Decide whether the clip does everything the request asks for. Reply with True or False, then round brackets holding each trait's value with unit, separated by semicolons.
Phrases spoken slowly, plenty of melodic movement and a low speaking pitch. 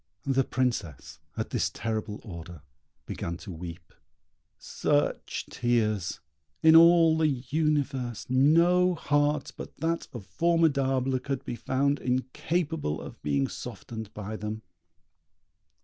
True (115 wpm; 6.1 semitones; 130 Hz)